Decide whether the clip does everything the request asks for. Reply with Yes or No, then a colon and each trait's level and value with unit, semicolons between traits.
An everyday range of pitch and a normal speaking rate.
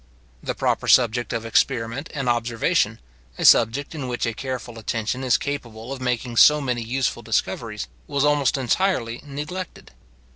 Yes: average, 3.4 semitones; average, 150 wpm